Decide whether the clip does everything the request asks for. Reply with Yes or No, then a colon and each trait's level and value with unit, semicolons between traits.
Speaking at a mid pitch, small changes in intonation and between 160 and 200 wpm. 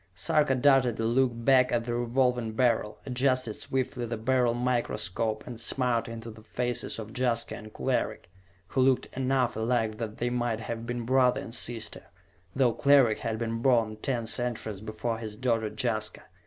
No: low, 120 Hz; narrow, 2.2 semitones; average, 170 wpm